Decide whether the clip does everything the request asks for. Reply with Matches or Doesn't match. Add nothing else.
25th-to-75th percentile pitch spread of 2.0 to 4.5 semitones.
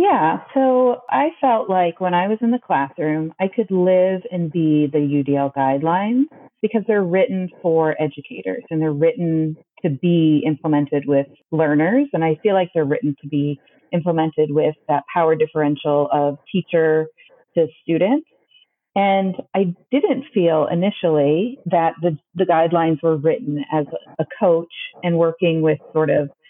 Matches